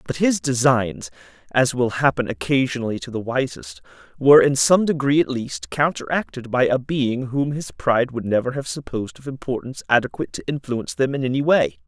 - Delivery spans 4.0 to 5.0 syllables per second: No, 5.6 syllables/s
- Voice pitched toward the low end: Yes, low, 130 Hz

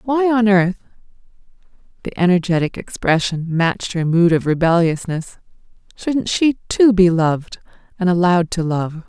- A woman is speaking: Yes, female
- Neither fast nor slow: No, slow, 120 wpm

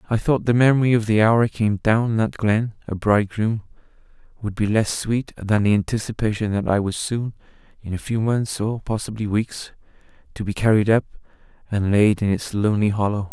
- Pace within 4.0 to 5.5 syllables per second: Yes, 5.4 syllables/s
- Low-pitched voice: Yes, low, 110 Hz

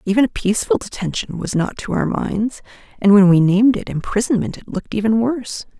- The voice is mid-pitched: No, high, 210 Hz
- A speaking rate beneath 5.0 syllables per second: No, 6.0 syllables/s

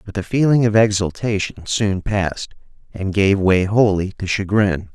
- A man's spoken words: Yes, male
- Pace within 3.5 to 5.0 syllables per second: Yes, 4.6 syllables/s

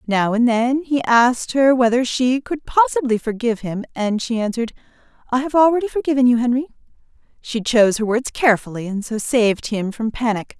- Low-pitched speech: No, high, 240 Hz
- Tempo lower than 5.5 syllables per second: No, 5.7 syllables/s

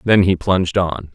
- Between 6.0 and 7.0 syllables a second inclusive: No, 4.8 syllables/s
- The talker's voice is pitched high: No, very low, 90 Hz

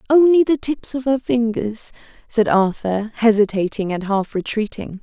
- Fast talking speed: No, average, 145 wpm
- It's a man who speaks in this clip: No, female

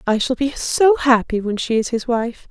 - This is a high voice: Yes, high, 245 Hz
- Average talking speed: No, fast, 240 wpm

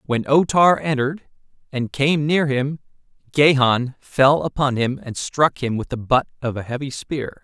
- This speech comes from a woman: No, male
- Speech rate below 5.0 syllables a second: Yes, 4.4 syllables/s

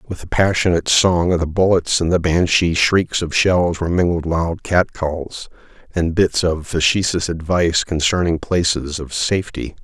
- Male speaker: Yes, male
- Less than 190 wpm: Yes, average, 160 wpm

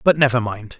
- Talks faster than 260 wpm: No, fast, 225 wpm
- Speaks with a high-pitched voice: No, low, 125 Hz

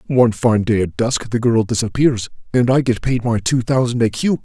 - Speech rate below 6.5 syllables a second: Yes, 5.0 syllables/s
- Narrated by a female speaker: No, male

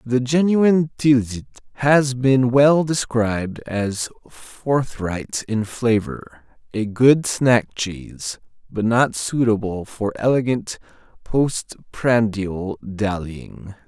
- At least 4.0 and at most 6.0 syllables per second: No, 3.1 syllables/s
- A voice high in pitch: No, low, 115 Hz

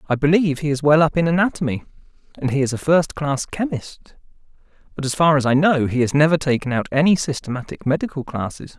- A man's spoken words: Yes, male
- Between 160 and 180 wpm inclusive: No, average, 200 wpm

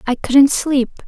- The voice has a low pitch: No, very high, 270 Hz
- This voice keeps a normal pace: Yes, average, 165 wpm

